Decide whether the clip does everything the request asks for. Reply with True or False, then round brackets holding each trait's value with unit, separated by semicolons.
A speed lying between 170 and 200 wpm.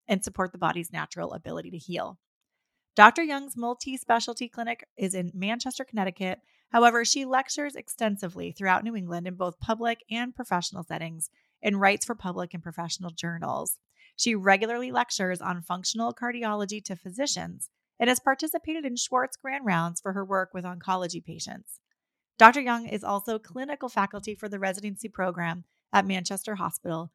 False (155 wpm)